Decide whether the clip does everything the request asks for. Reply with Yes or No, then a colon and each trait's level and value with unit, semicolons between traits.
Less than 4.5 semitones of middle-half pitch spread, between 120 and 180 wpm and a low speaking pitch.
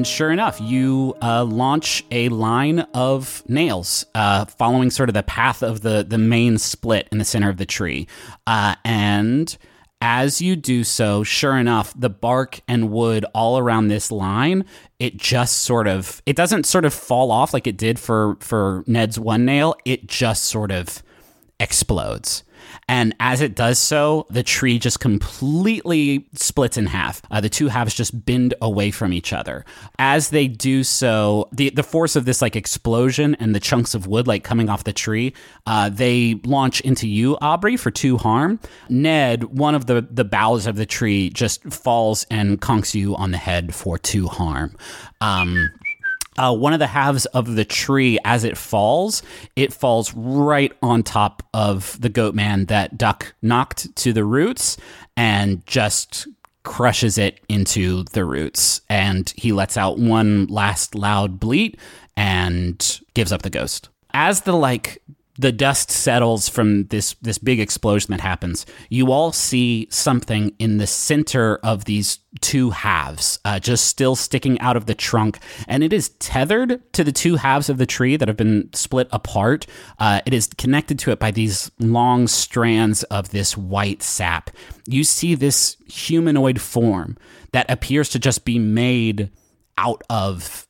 Yes: average, 4.0 semitones; average, 170 wpm; low, 115 Hz